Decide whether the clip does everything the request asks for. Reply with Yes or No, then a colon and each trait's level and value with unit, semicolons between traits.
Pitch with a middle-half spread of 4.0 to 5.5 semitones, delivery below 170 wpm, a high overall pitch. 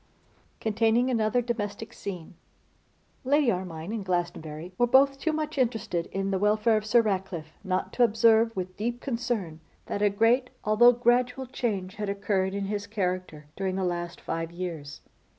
Yes: average, 4.4 semitones; average, 160 wpm; high, 210 Hz